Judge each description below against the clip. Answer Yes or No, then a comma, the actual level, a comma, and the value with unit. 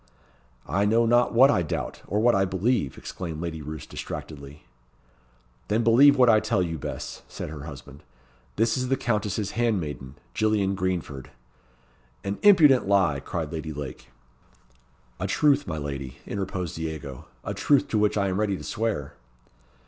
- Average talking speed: Yes, average, 155 wpm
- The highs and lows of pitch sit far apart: Yes, wide, 6.9 semitones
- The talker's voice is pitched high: No, very low, 95 Hz